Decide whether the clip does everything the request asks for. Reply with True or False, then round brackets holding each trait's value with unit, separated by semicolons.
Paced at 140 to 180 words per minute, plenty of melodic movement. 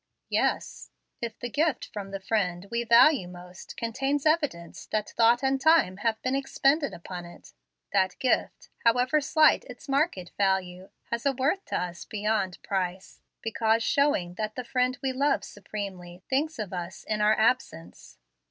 True (160 wpm; 6.2 semitones)